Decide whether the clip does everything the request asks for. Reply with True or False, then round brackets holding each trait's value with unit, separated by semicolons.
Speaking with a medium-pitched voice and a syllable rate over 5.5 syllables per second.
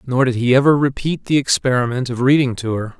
False (130 Hz; 5.9 syllables/s)